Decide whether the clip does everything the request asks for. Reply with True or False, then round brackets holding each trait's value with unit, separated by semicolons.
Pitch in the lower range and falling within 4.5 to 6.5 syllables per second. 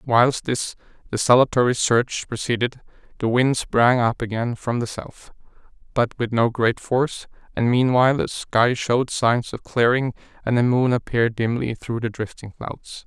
True (120 Hz; 4.6 syllables/s)